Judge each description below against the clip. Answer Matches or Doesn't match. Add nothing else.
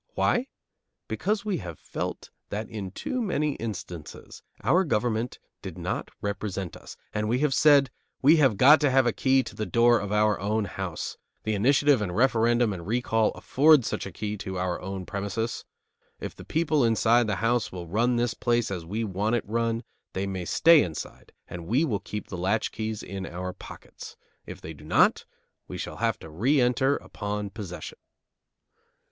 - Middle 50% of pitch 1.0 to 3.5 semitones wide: Doesn't match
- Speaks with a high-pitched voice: Doesn't match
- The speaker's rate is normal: Matches